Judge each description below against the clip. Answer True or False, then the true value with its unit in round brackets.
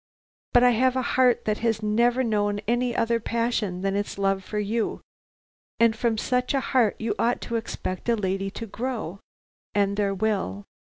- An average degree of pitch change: True (3.0 semitones)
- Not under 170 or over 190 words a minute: True (180 wpm)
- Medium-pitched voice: False (220 Hz)